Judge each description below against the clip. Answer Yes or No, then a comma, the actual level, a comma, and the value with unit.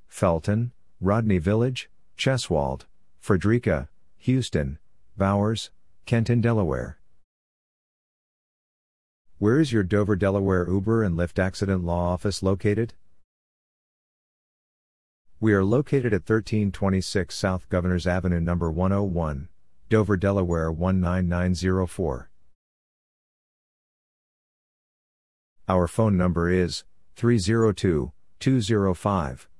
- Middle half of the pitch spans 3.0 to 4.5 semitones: Yes, average, 3.5 semitones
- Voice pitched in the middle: No, very low, 95 Hz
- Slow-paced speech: Yes, slow, 80 wpm